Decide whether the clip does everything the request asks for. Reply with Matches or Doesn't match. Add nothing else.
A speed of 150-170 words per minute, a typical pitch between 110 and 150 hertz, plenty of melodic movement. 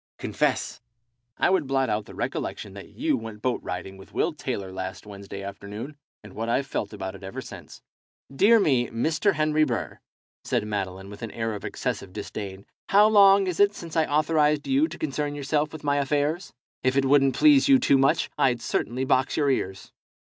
Doesn't match